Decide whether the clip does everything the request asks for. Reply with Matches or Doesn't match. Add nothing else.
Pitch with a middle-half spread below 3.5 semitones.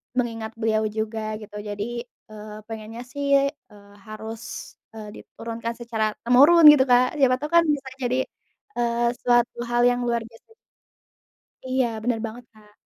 Matches